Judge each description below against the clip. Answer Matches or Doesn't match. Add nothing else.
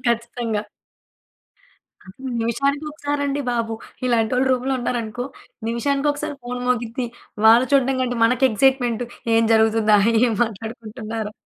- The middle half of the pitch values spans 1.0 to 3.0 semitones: Matches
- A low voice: Doesn't match